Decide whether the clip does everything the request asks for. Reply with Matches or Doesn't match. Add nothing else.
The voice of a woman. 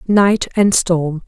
Matches